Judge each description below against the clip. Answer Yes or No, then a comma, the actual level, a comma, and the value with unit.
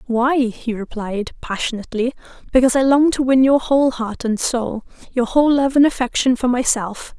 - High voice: Yes, high, 245 Hz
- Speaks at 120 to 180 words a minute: Yes, average, 175 wpm